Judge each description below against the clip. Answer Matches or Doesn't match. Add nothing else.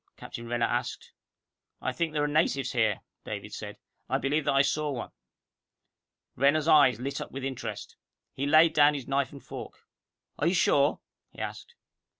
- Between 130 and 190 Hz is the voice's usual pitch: Matches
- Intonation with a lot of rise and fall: Doesn't match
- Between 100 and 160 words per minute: Doesn't match